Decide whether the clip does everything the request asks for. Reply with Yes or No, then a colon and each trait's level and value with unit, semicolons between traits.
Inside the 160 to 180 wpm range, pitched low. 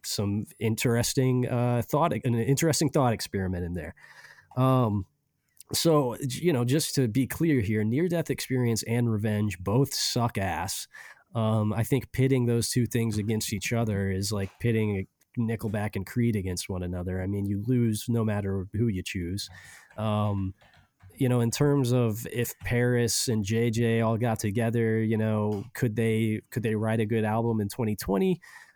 Yes: average, 170 wpm; low, 115 Hz